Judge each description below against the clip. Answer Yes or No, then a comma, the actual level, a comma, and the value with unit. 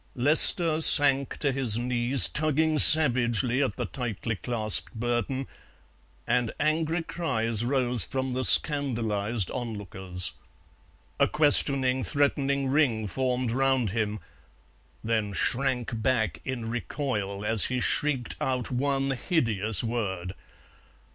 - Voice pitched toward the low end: Yes, low, 125 Hz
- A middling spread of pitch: Yes, average, 3.6 semitones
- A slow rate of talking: Yes, slow, 110 wpm